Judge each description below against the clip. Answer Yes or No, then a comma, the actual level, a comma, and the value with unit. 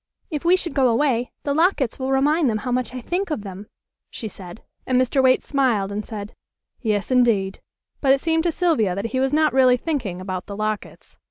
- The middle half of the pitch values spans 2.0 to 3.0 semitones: No, average, 5.2 semitones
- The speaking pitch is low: No, very high, 255 Hz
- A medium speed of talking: No, fast, 210 wpm